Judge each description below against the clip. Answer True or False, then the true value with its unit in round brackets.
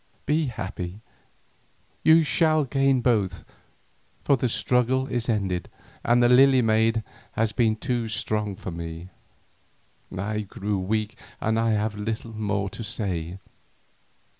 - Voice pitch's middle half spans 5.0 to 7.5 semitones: False (3.6 semitones)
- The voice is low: True (110 Hz)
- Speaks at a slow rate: True (130 wpm)